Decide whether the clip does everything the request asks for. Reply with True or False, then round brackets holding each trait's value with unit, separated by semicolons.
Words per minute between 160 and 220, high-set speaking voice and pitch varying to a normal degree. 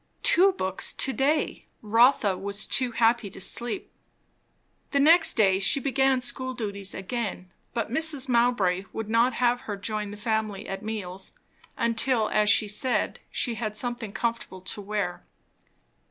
False (150 wpm; 225 Hz; 3.8 semitones)